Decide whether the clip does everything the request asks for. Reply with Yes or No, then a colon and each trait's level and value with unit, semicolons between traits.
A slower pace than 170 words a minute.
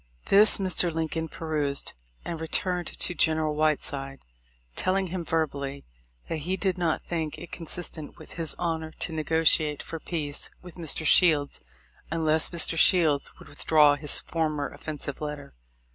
Yes: average, 145 wpm